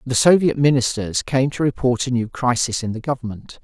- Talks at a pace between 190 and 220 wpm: Yes, average, 200 wpm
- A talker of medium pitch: No, low, 125 Hz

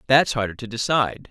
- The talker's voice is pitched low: Yes, low, 120 Hz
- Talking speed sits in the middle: Yes, average, 185 wpm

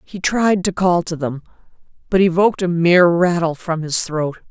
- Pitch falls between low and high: Yes, medium, 175 Hz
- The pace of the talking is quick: No, average, 185 wpm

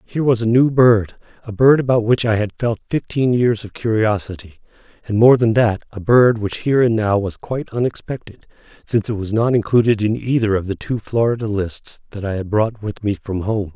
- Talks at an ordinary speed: No, fast, 215 wpm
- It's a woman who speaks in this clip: No, male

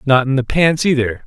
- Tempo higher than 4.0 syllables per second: Yes, 5.3 syllables/s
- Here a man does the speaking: Yes, male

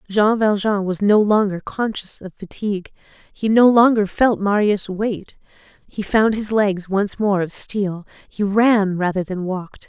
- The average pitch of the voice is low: No, high, 205 Hz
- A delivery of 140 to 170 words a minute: Yes, average, 165 wpm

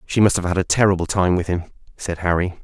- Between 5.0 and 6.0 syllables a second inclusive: No, 6.4 syllables/s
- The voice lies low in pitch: Yes, very low, 90 Hz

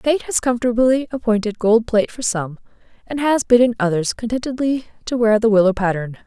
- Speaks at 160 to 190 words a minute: Yes, average, 170 wpm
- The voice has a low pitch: No, high, 230 Hz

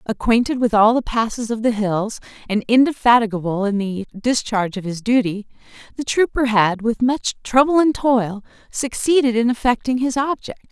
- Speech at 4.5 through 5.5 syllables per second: Yes, 5.0 syllables/s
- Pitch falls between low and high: No, high, 230 Hz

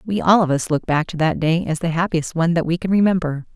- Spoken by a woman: Yes, female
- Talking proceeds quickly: Yes, fast, 285 wpm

